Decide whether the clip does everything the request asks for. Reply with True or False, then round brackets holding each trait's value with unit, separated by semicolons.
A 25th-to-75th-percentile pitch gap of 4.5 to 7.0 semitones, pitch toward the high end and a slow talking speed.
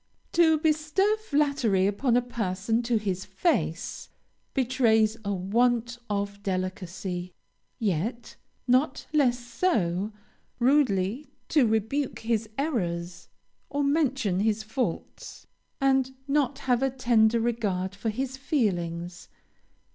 True (5.3 semitones; 230 Hz; 110 wpm)